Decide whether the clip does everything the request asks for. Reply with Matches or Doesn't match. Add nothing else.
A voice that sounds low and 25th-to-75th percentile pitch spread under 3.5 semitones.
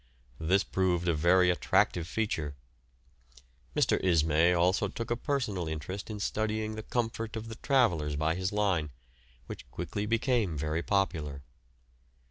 Doesn't match